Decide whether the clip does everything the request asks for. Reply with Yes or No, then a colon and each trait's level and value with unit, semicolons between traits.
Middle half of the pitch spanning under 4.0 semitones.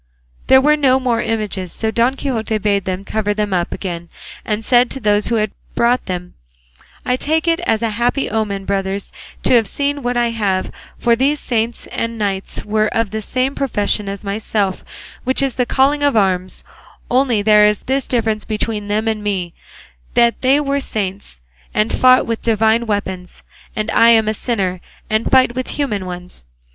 Yes: average, 3.6 semitones